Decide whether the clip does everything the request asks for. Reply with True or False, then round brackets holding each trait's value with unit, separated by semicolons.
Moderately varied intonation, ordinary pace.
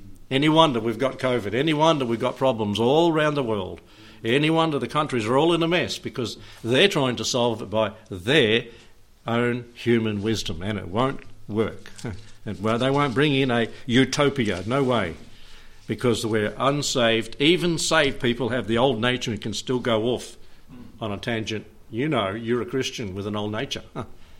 True (3.4 semitones; 190 wpm)